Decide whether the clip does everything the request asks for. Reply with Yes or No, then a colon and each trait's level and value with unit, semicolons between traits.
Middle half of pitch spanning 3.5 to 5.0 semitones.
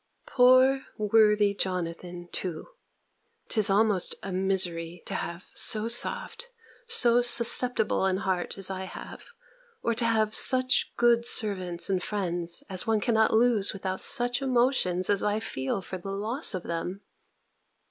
Yes: average, 4.3 semitones